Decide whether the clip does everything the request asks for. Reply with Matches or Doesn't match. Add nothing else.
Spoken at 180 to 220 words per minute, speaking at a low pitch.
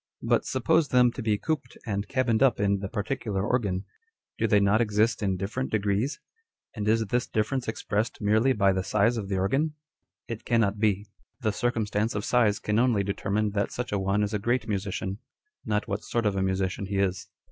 Matches